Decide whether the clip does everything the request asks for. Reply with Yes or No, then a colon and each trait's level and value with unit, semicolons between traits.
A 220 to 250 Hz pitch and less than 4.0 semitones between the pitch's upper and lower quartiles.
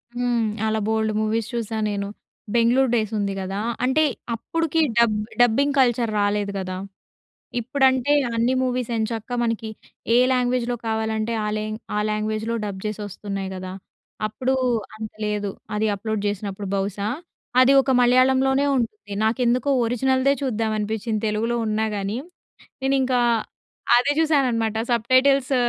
Yes: high, 225 Hz; average, 3.0 semitones